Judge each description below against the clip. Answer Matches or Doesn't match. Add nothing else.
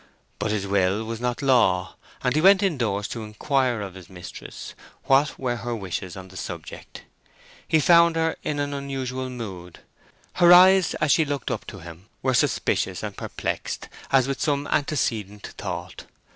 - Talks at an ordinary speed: Matches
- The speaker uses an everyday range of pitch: Doesn't match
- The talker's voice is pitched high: Doesn't match